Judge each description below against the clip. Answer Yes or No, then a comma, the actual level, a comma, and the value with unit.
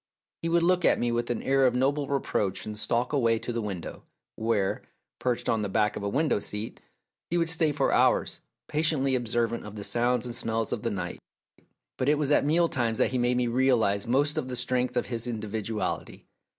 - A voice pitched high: No, low, 120 Hz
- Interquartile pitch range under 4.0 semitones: Yes, average, 3.5 semitones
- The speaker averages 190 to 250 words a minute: Yes, fast, 205 wpm